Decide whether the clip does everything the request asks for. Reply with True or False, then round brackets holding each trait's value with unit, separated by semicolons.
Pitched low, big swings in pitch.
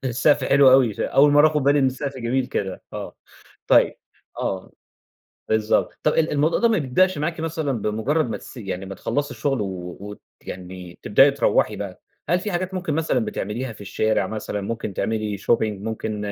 True (130 Hz; 6.0 semitones)